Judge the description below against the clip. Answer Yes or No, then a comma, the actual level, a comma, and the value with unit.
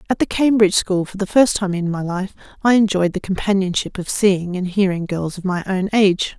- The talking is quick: Yes, fast, 225 wpm